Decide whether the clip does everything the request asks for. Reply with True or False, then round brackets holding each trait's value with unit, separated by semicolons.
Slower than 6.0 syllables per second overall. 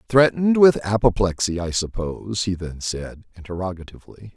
True (5.5 syllables/s)